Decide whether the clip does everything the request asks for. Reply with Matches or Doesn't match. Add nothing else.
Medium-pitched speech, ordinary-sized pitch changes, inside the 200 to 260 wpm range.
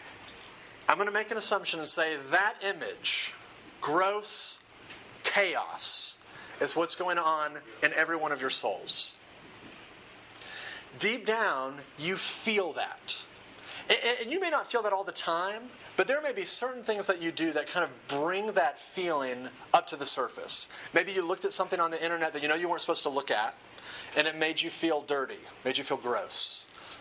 Doesn't match